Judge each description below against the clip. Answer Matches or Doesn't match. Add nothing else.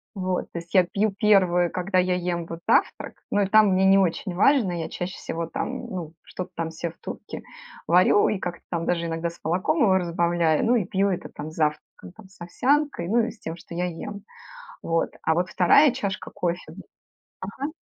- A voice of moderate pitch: Matches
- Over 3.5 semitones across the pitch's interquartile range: Doesn't match